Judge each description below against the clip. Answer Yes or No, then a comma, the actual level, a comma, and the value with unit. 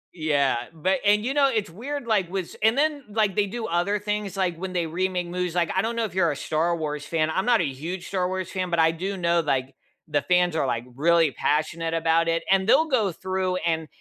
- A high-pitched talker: No, medium, 180 Hz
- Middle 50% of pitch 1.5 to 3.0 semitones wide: No, average, 3.7 semitones